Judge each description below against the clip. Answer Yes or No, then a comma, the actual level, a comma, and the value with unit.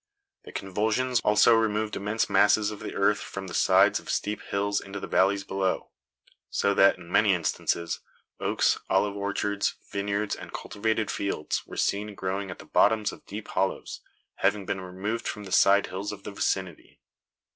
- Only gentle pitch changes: Yes, narrow, 1.6 semitones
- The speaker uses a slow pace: No, average, 170 wpm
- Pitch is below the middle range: Yes, low, 100 Hz